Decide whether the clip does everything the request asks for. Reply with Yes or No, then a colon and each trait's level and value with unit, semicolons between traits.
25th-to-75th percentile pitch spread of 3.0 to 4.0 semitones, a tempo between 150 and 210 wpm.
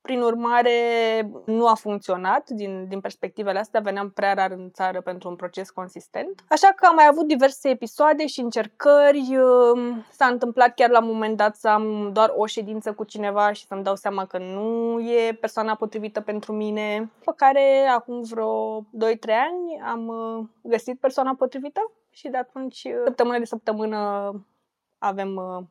Yes: average, 3.4 semitones; average, 165 wpm